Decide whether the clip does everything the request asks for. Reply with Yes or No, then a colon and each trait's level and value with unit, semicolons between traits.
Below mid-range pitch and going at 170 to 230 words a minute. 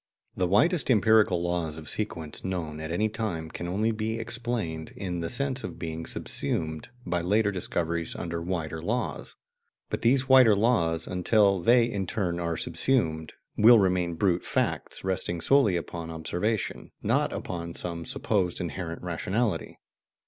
No: very low, 90 Hz; average, 150 wpm